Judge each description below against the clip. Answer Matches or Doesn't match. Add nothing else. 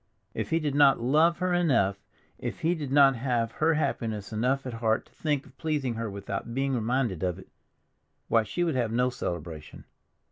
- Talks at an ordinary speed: Matches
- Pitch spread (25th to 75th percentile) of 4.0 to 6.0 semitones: Matches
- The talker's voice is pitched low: Matches